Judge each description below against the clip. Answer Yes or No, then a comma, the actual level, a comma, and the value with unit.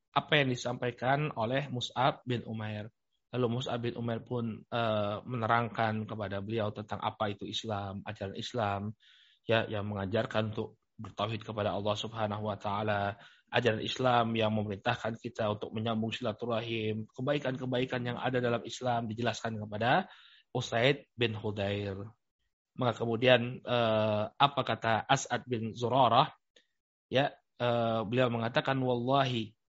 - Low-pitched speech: Yes, low, 115 Hz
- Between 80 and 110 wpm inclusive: No, average, 120 wpm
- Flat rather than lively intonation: Yes, narrow, 2.3 semitones